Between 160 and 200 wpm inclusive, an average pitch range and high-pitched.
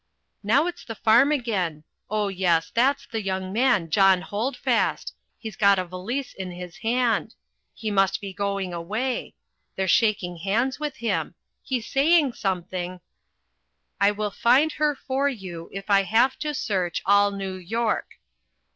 No: average, 150 wpm; average, 4.6 semitones; high, 205 Hz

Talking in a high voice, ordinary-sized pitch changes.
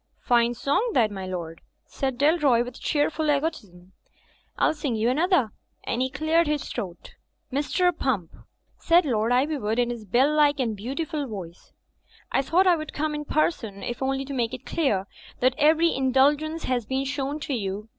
Yes: very high, 265 Hz; average, 4.7 semitones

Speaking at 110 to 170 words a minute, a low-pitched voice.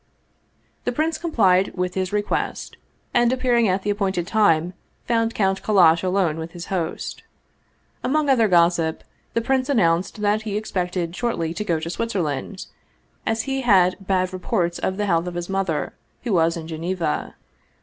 No: average, 165 wpm; high, 190 Hz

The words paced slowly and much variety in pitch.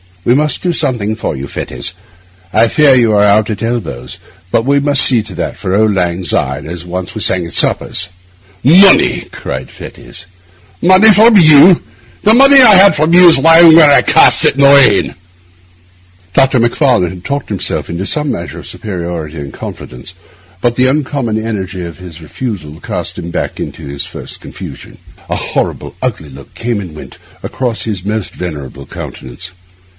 No: average, 180 wpm; wide, 8.4 semitones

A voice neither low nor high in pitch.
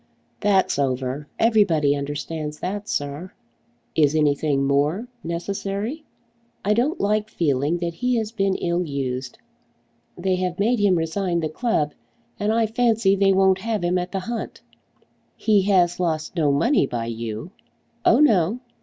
Yes: medium, 180 Hz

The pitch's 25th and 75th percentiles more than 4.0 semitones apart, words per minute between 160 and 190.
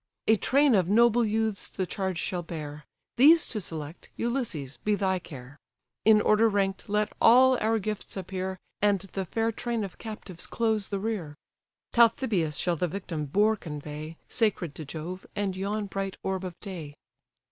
Yes: average, 4.4 semitones; average, 165 wpm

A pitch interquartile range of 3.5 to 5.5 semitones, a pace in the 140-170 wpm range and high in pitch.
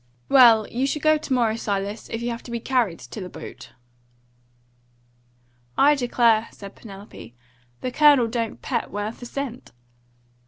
No: average, 3.0 semitones; average, 155 wpm; high, 235 Hz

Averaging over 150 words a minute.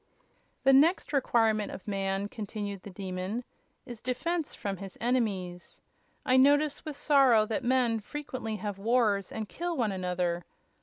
No: average, 145 wpm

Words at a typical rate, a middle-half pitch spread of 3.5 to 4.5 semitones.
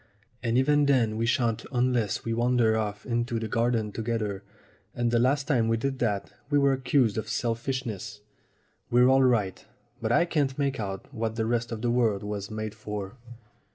No: average, 185 wpm; narrow, 2.6 semitones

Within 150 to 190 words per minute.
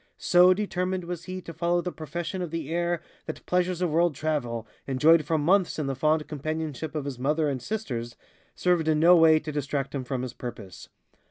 No: average, 200 wpm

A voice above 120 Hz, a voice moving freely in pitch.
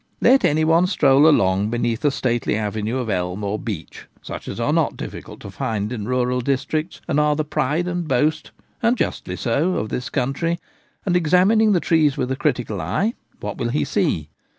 Yes: low, 135 Hz; wide, 6.5 semitones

